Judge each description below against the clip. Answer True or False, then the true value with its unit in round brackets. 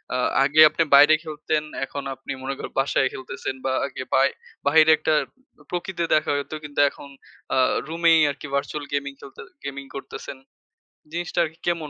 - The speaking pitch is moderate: True (145 Hz)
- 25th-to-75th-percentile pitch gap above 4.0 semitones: False (2.4 semitones)